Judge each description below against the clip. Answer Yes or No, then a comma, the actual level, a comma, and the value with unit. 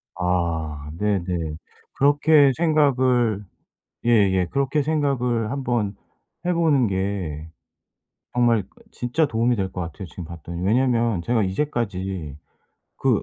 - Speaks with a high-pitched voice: No, low, 115 Hz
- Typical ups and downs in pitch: No, wide, 6.3 semitones